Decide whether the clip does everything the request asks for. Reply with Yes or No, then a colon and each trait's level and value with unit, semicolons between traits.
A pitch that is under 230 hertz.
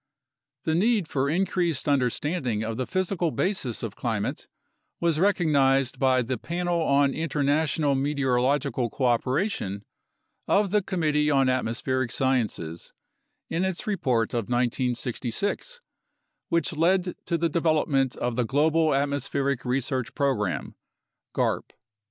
Yes: medium, 140 Hz